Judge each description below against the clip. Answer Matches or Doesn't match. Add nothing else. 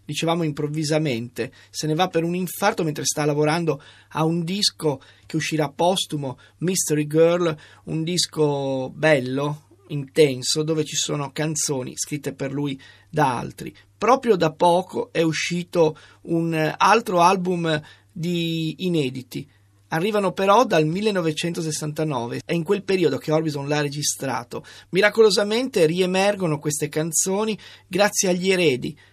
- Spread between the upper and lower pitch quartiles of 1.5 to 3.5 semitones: Matches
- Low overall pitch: Doesn't match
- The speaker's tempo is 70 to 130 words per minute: Matches